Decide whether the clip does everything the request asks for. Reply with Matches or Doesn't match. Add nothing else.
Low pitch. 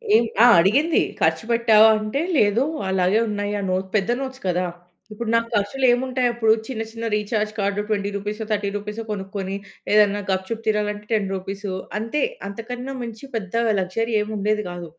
Doesn't match